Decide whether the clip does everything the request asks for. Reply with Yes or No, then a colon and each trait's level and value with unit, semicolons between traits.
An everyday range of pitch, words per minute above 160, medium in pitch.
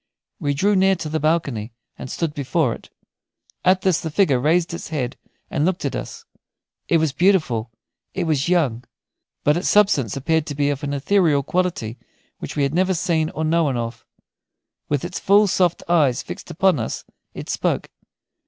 Yes: average, 4.1 semitones; average, 180 wpm; medium, 160 Hz